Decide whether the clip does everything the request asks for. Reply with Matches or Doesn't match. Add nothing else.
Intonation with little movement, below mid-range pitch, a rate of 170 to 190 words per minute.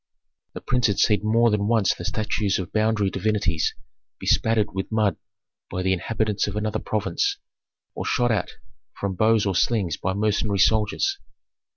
Doesn't match